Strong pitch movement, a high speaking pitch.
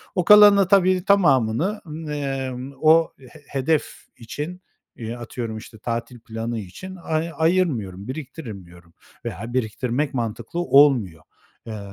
No: wide, 6.5 semitones; low, 130 Hz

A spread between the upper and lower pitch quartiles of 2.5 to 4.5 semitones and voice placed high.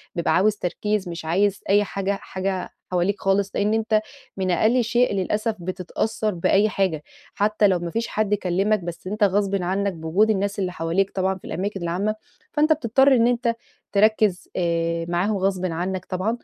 Yes: average, 2.8 semitones; high, 195 Hz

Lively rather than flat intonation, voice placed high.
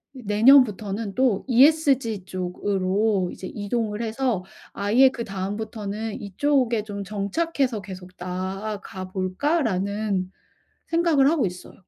No: average, 4.6 semitones; high, 210 Hz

